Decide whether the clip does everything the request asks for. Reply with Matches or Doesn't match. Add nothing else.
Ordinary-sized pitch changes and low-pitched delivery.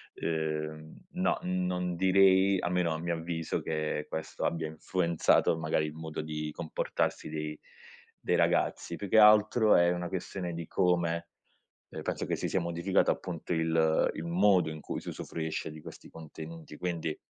Doesn't match